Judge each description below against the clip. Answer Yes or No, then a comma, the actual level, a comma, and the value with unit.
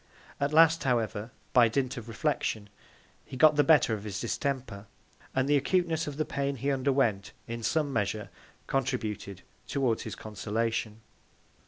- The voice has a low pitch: Yes, low, 125 Hz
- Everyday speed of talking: Yes, average, 150 wpm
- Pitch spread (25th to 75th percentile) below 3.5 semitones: No, average, 4.5 semitones